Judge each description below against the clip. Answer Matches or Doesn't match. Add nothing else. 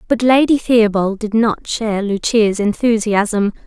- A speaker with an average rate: Doesn't match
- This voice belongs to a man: Doesn't match